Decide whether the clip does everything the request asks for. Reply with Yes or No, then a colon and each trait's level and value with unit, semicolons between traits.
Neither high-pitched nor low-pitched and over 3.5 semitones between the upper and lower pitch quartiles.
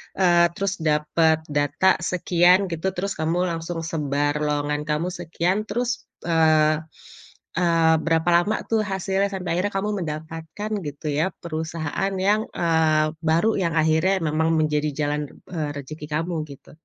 No: medium, 165 Hz; average, 2.9 semitones